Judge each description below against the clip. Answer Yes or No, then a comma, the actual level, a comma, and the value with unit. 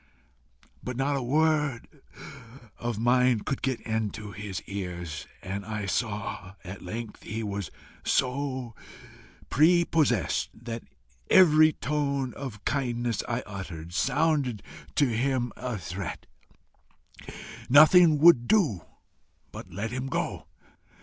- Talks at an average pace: No, slow, 115 wpm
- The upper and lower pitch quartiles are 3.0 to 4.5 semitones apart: No, wide, 5.5 semitones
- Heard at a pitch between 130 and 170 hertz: No, low, 120 Hz